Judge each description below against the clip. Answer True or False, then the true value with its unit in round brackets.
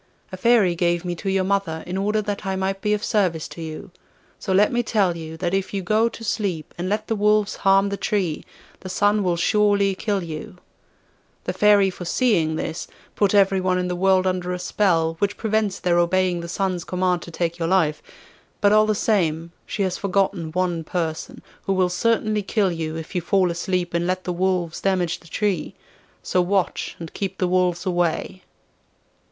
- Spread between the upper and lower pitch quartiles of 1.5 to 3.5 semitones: True (2.6 semitones)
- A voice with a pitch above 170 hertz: True (185 Hz)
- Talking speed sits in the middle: True (195 wpm)